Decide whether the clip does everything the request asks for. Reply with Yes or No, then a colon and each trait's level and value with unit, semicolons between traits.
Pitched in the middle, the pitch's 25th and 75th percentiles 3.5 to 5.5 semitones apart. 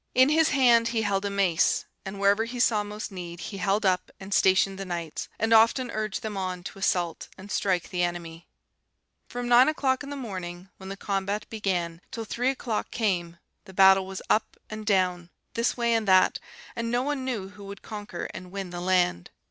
No: high, 200 Hz; average, 3.8 semitones